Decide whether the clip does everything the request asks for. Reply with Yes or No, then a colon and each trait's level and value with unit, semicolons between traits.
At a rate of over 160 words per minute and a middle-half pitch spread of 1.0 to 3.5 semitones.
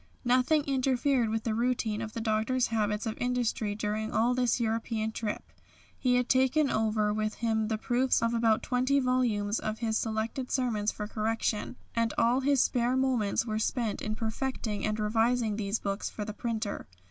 Yes: average, 175 wpm; narrow, 2.5 semitones